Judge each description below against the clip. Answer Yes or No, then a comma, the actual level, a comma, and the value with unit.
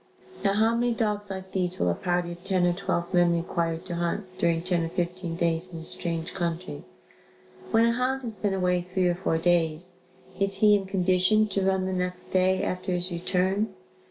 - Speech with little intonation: Yes, narrow, 2.1 semitones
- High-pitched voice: No, medium, 180 Hz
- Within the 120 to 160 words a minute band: No, fast, 205 wpm